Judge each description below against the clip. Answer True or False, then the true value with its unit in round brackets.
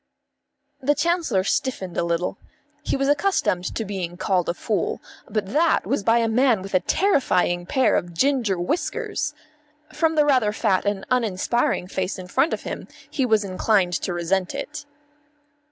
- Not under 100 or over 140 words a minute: False (165 wpm)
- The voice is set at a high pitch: True (210 Hz)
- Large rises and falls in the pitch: True (6.8 semitones)